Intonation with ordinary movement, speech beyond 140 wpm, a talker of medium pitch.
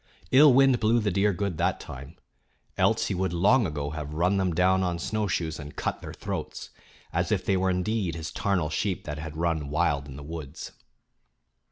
No: average, 4.5 semitones; average, 195 wpm; very low, 90 Hz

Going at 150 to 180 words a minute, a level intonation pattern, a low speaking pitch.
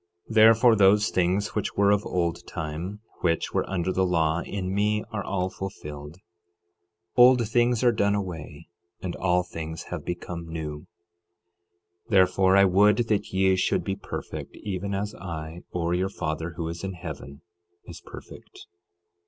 No: average, 160 wpm; average, 3.3 semitones; very low, 95 Hz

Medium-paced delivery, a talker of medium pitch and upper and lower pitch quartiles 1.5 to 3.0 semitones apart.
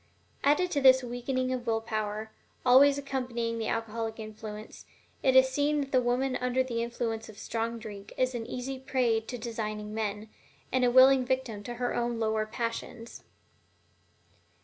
No: average, 170 wpm; high, 240 Hz; narrow, 2.6 semitones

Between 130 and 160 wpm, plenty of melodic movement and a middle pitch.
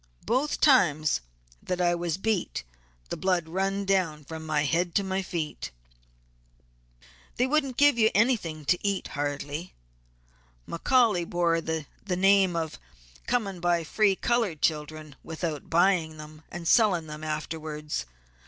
No: slow, 135 wpm; average, 4.1 semitones; medium, 175 Hz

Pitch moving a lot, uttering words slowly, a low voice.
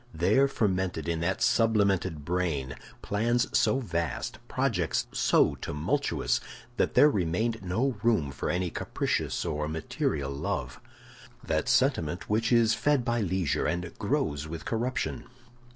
Yes: wide, 6.0 semitones; slow, 125 wpm; very low, 95 Hz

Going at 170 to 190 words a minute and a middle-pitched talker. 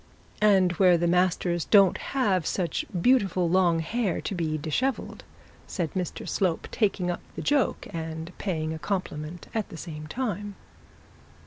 No: average, 145 wpm; medium, 180 Hz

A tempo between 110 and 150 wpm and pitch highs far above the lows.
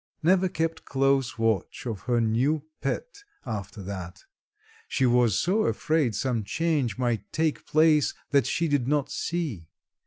Yes: average, 145 wpm; wide, 5.9 semitones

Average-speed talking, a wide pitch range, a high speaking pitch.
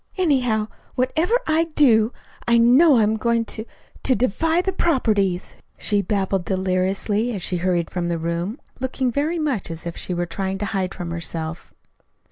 Yes: average, 165 wpm; wide, 5.9 semitones; high, 215 Hz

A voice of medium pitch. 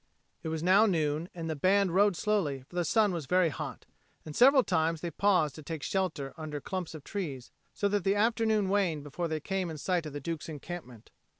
Yes: medium, 170 Hz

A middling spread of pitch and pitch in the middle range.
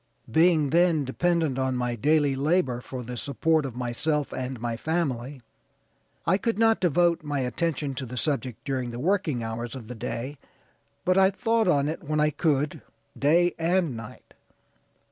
Yes: average, 4.9 semitones; medium, 145 Hz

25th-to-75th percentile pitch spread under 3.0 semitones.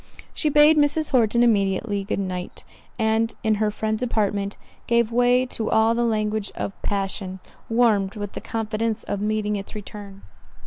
Yes: narrow, 2.6 semitones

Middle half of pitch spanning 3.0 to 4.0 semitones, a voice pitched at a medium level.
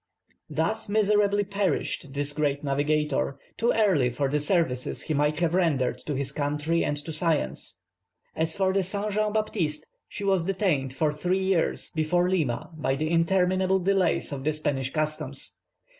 No: average, 4.7 semitones; medium, 160 Hz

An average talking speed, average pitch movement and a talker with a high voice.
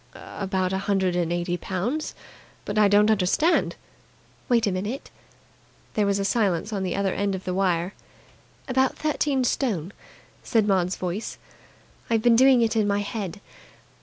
Yes: average, 160 wpm; average, 3.5 semitones; high, 200 Hz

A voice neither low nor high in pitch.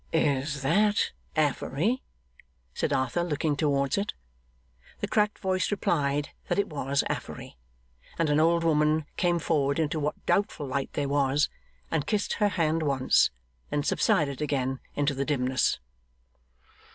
Yes: medium, 150 Hz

